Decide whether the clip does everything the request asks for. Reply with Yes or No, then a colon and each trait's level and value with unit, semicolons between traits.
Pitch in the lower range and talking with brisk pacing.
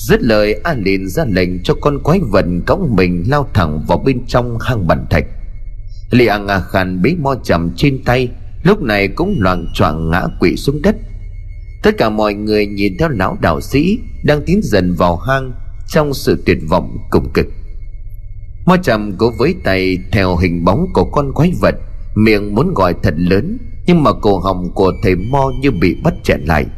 No: low, 100 Hz; average, 195 wpm